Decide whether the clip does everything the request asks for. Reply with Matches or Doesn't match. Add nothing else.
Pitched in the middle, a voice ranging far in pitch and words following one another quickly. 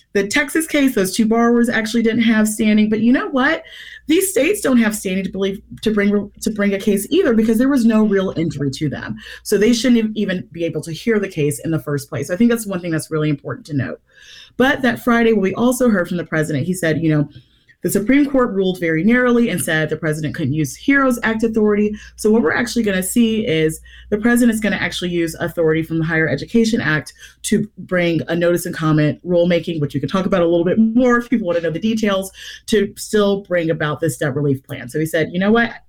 Doesn't match